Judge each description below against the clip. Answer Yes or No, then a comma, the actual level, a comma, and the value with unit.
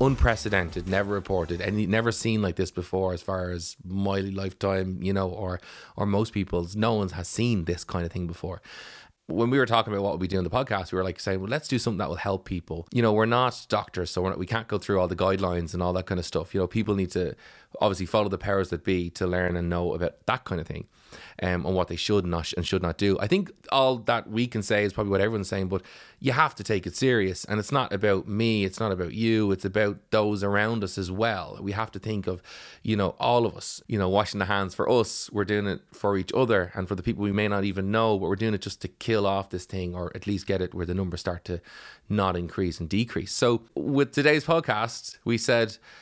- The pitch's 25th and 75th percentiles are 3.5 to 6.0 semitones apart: No, average, 3.0 semitones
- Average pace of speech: No, fast, 260 wpm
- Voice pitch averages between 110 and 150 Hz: No, low, 100 Hz